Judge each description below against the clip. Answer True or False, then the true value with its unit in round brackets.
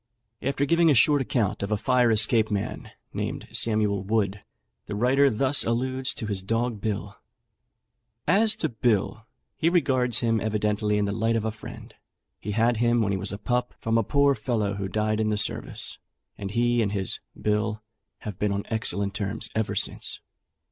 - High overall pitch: False (110 Hz)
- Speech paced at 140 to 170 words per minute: False (180 wpm)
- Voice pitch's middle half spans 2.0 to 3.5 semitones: True (2.9 semitones)